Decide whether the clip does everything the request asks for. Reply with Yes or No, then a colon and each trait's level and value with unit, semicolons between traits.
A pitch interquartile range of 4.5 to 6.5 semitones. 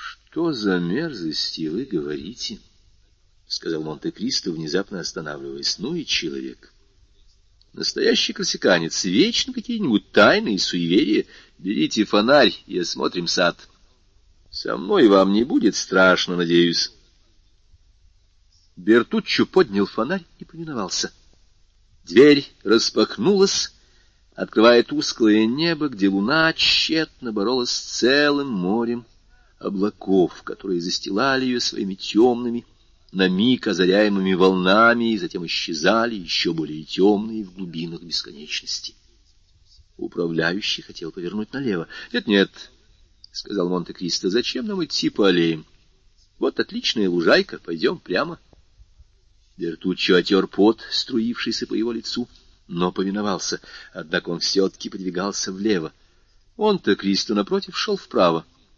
Yes: average, 5.1 semitones